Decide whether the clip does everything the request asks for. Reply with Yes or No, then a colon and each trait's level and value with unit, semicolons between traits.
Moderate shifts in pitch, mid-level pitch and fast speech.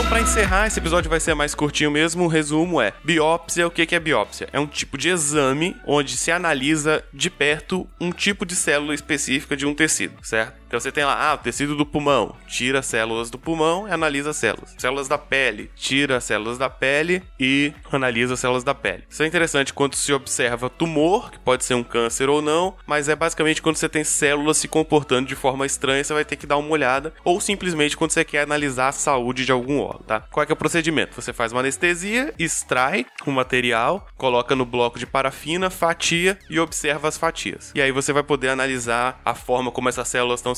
Yes: average, 3.7 semitones; medium, 145 Hz; fast, 225 wpm